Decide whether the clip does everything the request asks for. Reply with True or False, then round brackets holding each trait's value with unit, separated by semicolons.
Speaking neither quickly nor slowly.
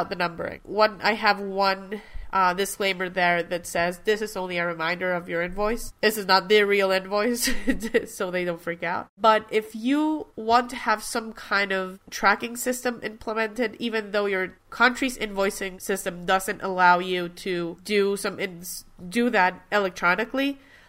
True (165 wpm)